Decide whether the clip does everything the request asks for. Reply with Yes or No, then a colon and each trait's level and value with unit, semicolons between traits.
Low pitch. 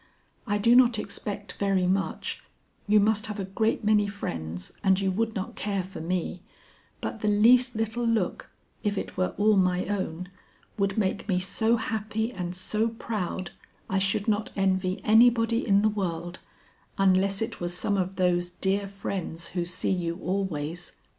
No: high, 195 Hz